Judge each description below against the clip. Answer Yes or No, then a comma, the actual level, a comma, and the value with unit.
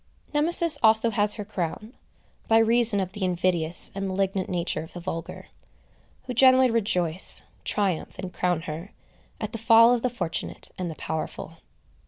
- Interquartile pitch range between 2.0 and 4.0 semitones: No, average, 4.5 semitones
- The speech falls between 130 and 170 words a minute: Yes, average, 160 wpm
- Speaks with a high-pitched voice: Yes, high, 195 Hz